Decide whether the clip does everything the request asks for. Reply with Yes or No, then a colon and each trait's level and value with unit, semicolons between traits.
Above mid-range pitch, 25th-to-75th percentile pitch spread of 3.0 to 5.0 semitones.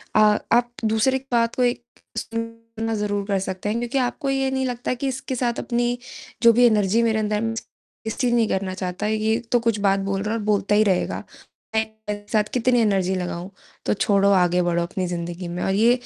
Yes: high, 220 Hz; average, 3.5 semitones